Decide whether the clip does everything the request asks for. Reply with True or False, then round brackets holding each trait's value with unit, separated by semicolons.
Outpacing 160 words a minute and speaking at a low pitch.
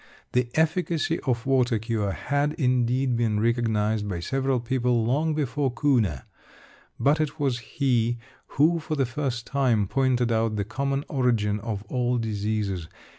False (145 wpm; 125 Hz)